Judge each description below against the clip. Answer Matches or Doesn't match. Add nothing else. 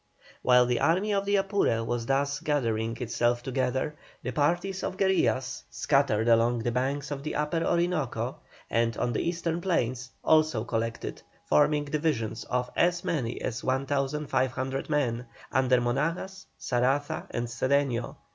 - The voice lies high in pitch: Doesn't match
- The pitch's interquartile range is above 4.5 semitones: Doesn't match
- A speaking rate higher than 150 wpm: Doesn't match